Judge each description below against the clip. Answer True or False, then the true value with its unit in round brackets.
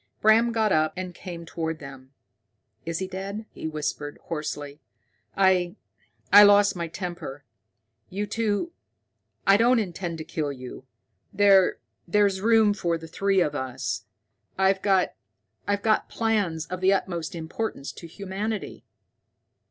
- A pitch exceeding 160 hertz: True (185 Hz)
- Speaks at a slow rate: True (130 wpm)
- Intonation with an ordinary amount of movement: True (4.1 semitones)